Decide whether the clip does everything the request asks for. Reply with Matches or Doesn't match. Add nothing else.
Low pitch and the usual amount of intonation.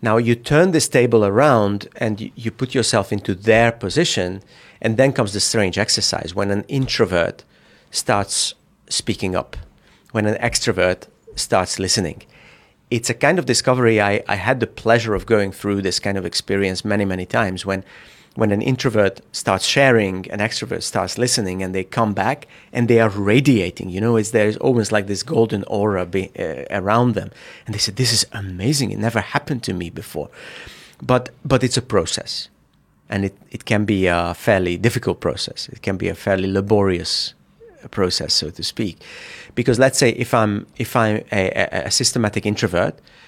Matches